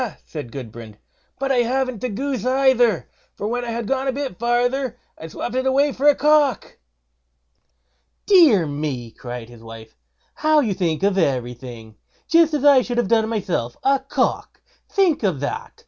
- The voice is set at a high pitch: Yes, high, 235 Hz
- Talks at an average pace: Yes, average, 170 wpm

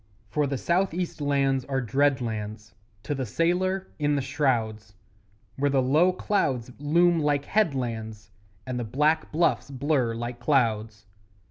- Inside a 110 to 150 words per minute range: Yes, average, 145 wpm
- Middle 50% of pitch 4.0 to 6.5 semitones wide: Yes, average, 4.5 semitones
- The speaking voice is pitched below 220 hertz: Yes, low, 135 Hz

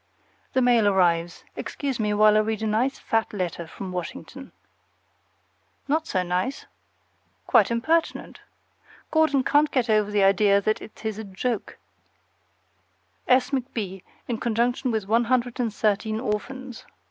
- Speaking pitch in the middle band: No, high, 220 Hz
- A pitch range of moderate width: Yes, average, 3.9 semitones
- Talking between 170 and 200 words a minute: No, average, 140 wpm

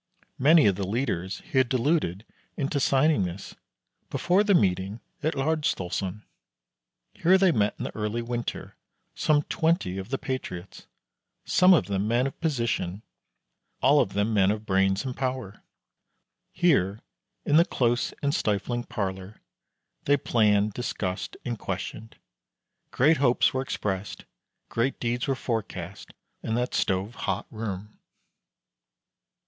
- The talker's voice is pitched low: Yes, low, 115 Hz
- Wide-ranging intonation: Yes, wide, 5.7 semitones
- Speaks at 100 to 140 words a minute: Yes, slow, 135 wpm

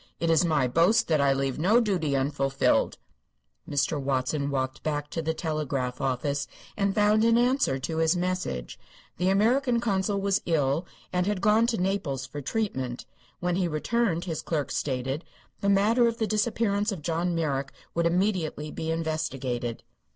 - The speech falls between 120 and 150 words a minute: No, average, 165 wpm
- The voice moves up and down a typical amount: No, wide, 6.2 semitones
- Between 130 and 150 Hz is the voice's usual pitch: No, medium, 165 Hz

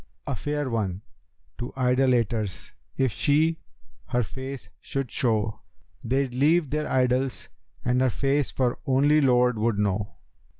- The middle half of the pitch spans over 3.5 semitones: No, average, 2.8 semitones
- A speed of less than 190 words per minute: Yes, slow, 135 wpm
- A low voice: Yes, low, 130 Hz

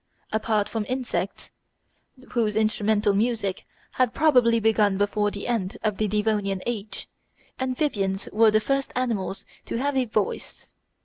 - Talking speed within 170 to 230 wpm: No, slow, 135 wpm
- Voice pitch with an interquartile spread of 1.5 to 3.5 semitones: Yes, average, 2.8 semitones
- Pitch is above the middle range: Yes, high, 215 Hz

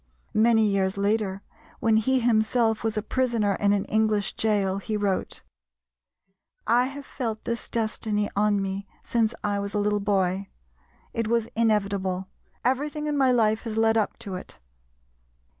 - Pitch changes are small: Yes, narrow, 2.3 semitones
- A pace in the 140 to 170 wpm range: Yes, average, 155 wpm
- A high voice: Yes, high, 215 Hz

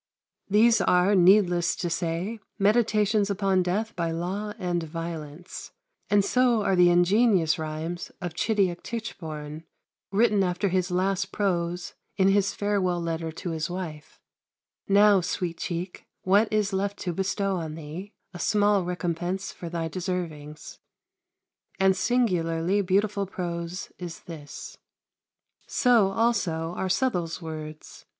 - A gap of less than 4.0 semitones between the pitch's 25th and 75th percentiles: Yes, average, 3.1 semitones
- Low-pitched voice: No, medium, 180 Hz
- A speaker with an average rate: No, slow, 130 wpm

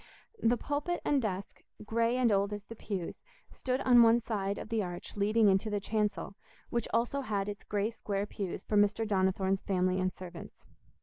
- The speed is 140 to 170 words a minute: No, average, 185 wpm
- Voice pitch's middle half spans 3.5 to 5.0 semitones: No, average, 2.9 semitones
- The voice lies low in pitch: No, high, 210 Hz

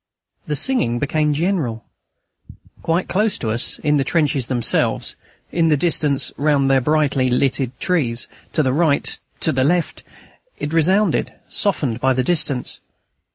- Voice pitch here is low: No, medium, 145 Hz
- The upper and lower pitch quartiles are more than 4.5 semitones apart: No, average, 4.0 semitones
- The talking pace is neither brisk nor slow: Yes, average, 145 wpm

